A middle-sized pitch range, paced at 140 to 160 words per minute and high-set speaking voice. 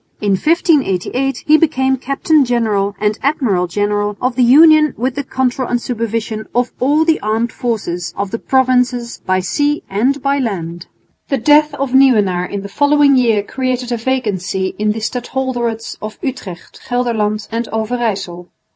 Yes: average, 4.2 semitones; average, 155 wpm; high, 240 Hz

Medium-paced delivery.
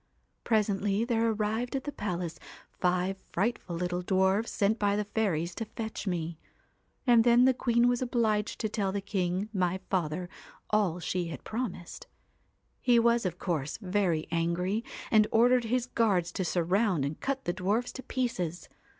Yes: average, 165 wpm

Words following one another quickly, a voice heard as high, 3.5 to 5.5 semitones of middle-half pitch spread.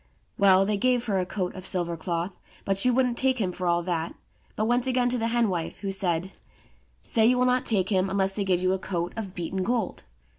Yes: fast, 235 wpm; high, 195 Hz; average, 4.4 semitones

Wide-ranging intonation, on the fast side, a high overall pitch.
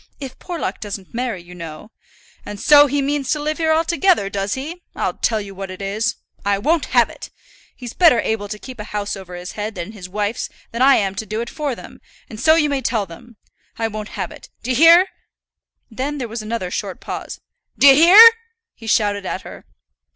Yes: wide, 6.0 semitones; fast, 215 wpm; high, 225 Hz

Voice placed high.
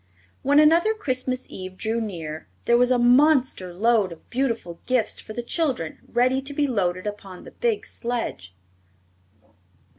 Yes: high, 240 Hz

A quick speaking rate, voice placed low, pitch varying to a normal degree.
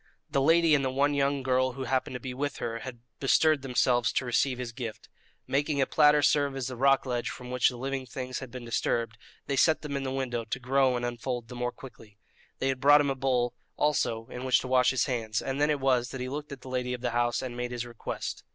No: fast, 255 wpm; low, 130 Hz; narrow, 2.0 semitones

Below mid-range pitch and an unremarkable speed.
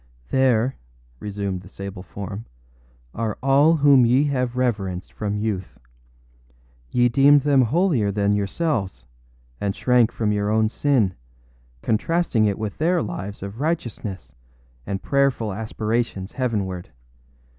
No: low, 110 Hz; slow, 125 wpm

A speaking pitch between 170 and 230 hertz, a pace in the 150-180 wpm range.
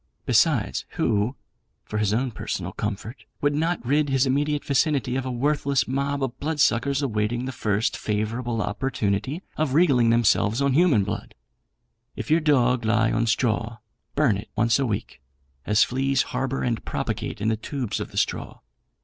No: low, 125 Hz; average, 165 wpm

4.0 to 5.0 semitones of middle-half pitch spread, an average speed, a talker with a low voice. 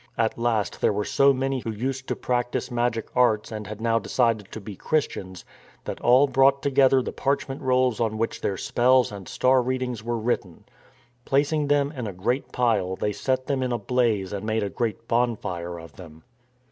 No: average, 3.5 semitones; average, 195 wpm; low, 120 Hz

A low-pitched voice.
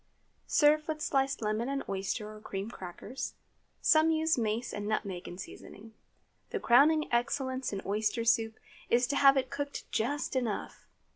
No: high, 240 Hz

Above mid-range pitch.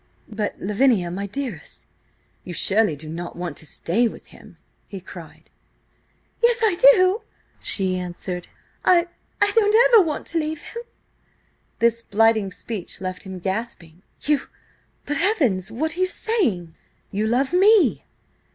Yes: high, 225 Hz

